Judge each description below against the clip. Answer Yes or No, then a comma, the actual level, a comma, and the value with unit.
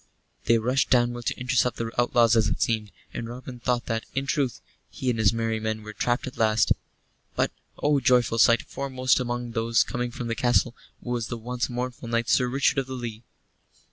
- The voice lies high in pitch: No, low, 120 Hz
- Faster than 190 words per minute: Yes, average, 200 wpm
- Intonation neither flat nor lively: No, narrow, 1.6 semitones